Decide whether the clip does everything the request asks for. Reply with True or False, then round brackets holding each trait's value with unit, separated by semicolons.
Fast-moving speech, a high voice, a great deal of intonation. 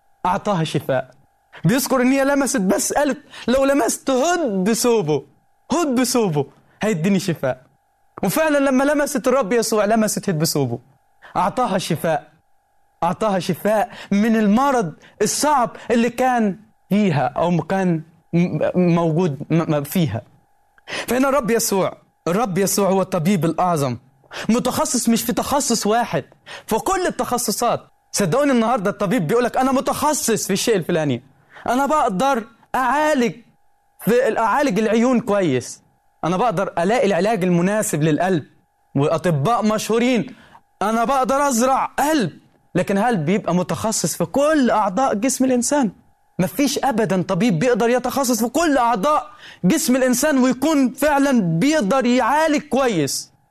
False (120 wpm; 225 Hz; 6.6 semitones)